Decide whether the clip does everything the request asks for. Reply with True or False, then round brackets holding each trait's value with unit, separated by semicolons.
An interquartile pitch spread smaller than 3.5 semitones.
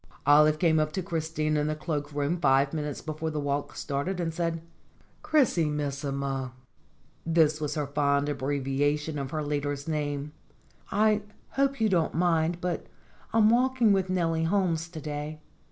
True (2.9 semitones)